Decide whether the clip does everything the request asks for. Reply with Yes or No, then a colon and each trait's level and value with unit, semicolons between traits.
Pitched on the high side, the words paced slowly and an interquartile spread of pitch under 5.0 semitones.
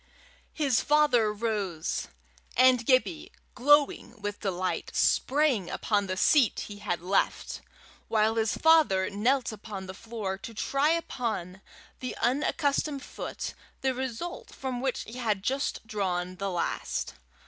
No: high, 230 Hz; slow, 130 wpm; average, 5.3 semitones